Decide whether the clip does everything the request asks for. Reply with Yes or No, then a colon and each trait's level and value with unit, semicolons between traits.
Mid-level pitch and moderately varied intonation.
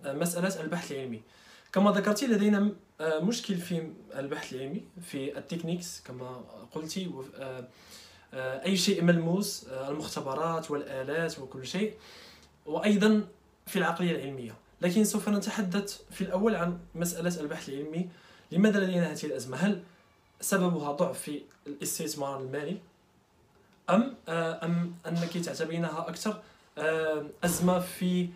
Yes: medium, 170 Hz; average, 4.7 semitones